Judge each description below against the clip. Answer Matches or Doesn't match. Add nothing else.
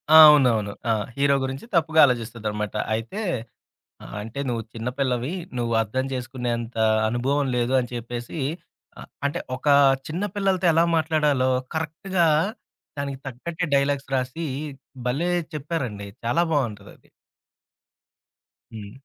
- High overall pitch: Doesn't match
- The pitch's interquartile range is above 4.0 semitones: Matches